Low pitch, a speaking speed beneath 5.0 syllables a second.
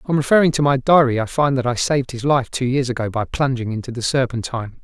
No: low, 130 Hz; 6.3 syllables/s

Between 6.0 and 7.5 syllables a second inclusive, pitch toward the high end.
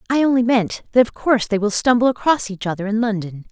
Yes: 6.3 syllables/s; high, 225 Hz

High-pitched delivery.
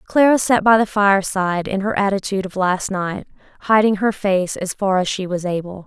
Yes: high, 195 Hz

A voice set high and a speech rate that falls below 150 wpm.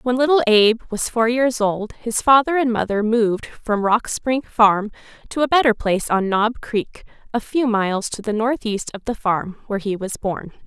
No: high, 225 Hz; average, 200 wpm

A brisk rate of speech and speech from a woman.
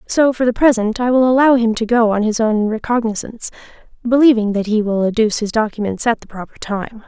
Yes: fast, 210 wpm; female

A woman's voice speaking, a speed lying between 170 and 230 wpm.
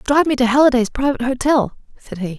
Yes: female; average, 200 wpm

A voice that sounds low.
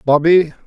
No: medium, 155 Hz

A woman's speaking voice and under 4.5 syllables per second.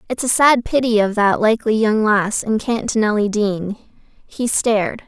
Yes: female; 4.3 syllables/s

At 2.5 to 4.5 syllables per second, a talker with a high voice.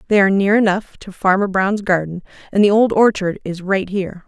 No: 5.6 syllables/s; high, 195 Hz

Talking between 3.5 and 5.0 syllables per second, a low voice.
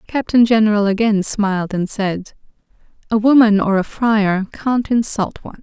No: 4.9 syllables/s; high, 215 Hz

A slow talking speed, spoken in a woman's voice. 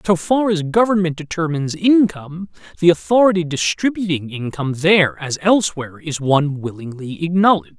No: slow, 130 wpm; male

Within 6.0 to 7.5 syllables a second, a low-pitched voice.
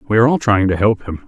Yes: 7.4 syllables/s; low, 105 Hz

